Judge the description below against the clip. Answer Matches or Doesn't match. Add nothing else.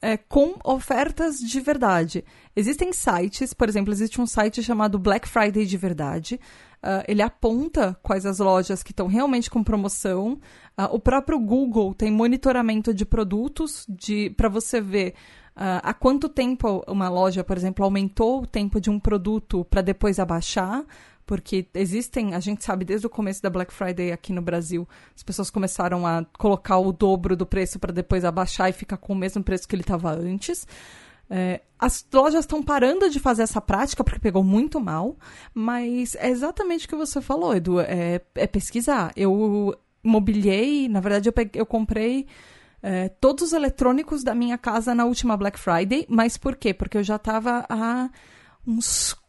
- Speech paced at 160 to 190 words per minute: Matches